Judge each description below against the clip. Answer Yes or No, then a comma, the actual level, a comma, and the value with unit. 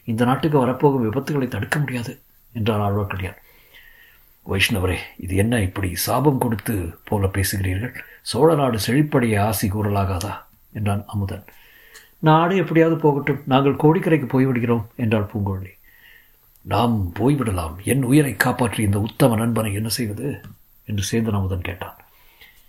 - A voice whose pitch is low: Yes, low, 115 Hz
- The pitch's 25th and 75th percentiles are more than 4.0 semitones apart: Yes, average, 4.5 semitones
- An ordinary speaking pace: Yes, average, 120 wpm